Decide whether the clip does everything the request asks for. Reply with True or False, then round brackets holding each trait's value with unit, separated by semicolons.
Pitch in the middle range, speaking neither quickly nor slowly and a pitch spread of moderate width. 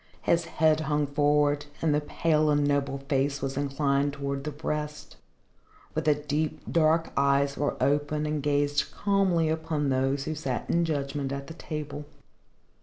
False (145 Hz; 160 wpm; 1.7 semitones)